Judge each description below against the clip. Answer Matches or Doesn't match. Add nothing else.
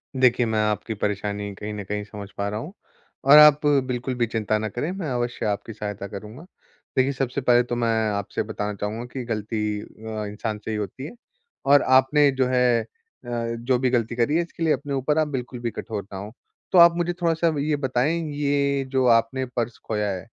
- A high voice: Doesn't match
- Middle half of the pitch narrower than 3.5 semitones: Doesn't match